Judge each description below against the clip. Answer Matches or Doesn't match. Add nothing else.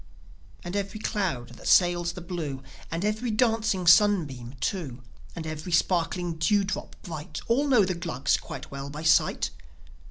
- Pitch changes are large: Doesn't match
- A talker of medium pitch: Matches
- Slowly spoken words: Doesn't match